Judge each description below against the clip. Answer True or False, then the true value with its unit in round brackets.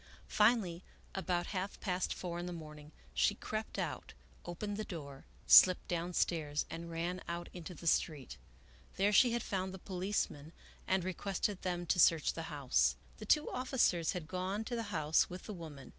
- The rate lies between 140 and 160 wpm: False (175 wpm)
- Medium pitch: True (180 Hz)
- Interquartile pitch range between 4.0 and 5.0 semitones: False (3.0 semitones)